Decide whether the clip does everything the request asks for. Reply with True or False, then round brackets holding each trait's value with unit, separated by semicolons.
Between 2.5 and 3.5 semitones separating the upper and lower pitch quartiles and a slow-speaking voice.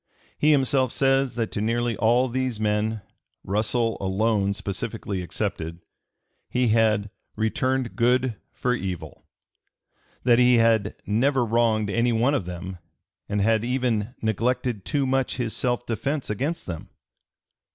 True (3.2 semitones; 130 wpm)